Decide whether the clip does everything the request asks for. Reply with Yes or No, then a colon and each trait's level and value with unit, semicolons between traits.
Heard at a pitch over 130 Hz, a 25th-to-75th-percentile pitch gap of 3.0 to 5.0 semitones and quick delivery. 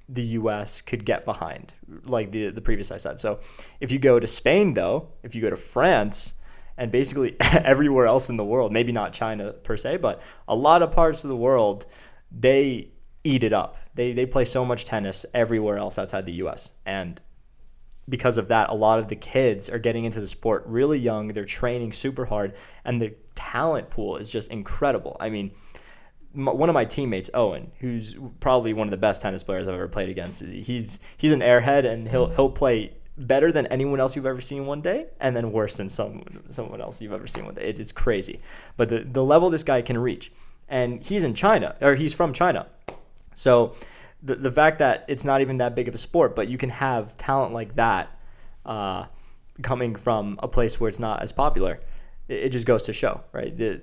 No: low, 125 Hz; average, 3.3 semitones; fast, 210 wpm